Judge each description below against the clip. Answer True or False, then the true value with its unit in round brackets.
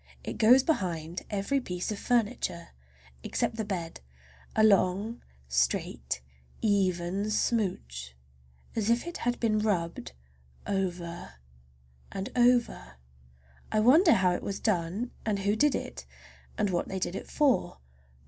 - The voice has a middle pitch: False (200 Hz)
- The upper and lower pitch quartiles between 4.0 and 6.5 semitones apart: True (4.8 semitones)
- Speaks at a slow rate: True (130 wpm)